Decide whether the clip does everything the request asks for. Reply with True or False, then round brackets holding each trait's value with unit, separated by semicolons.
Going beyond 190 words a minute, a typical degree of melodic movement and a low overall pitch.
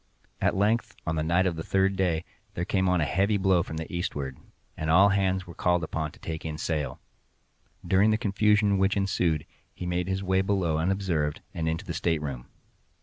True (200 wpm; 3.2 semitones; 90 Hz)